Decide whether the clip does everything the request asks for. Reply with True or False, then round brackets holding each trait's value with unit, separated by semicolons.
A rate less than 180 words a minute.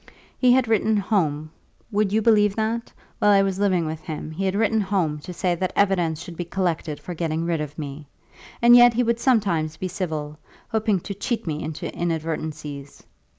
False (195 wpm)